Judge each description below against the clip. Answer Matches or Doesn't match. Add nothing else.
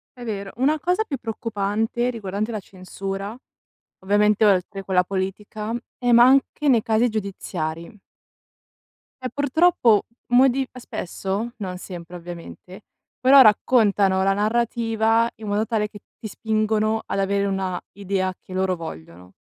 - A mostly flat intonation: Doesn't match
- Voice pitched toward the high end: Matches